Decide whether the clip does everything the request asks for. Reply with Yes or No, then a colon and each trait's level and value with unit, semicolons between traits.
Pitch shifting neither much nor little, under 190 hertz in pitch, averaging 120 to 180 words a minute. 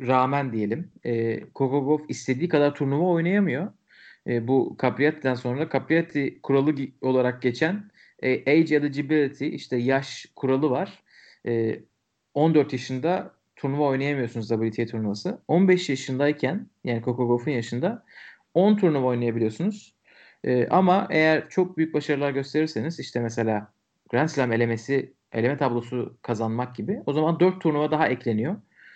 Yes: average, 4.3 semitones; low, 135 Hz; average, 130 wpm